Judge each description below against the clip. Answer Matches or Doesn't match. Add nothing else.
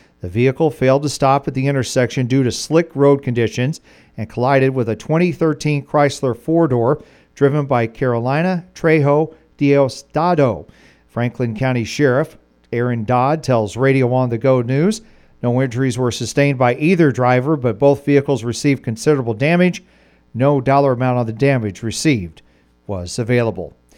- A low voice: Matches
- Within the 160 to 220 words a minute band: Doesn't match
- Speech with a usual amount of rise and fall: Matches